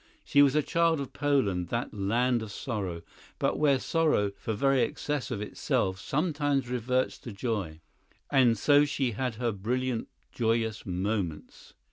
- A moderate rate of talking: Yes, average, 150 wpm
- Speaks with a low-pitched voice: Yes, low, 120 Hz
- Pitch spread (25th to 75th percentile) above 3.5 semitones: Yes, average, 5.1 semitones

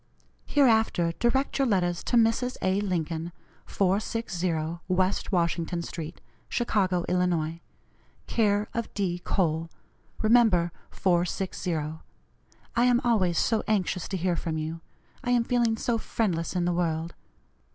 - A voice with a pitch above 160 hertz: Yes, medium, 185 Hz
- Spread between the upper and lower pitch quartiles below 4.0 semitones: No, average, 4.7 semitones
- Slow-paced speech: Yes, slow, 125 wpm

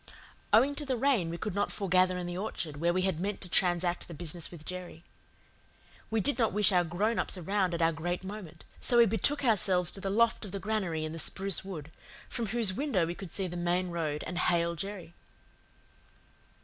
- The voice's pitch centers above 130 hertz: Yes, medium, 185 Hz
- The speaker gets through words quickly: Yes, fast, 215 wpm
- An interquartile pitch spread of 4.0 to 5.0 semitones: No, average, 3.3 semitones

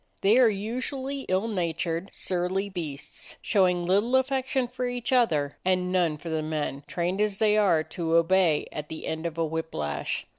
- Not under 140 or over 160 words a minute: No, average, 180 wpm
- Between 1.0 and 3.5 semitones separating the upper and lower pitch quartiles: No, average, 5.1 semitones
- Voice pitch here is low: No, medium, 185 Hz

